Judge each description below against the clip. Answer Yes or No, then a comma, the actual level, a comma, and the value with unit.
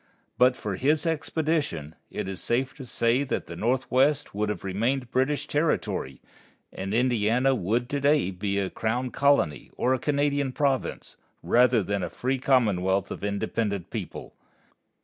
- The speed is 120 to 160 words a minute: Yes, average, 155 wpm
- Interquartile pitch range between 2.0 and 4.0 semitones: No, wide, 5.4 semitones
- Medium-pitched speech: No, low, 125 Hz